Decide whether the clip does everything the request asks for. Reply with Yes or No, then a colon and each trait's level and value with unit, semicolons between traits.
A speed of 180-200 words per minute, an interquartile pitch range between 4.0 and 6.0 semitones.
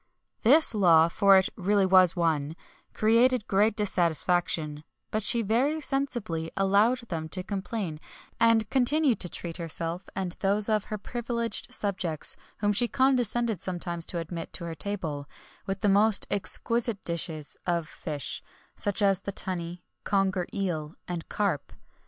No: average, 145 wpm; average, 4.5 semitones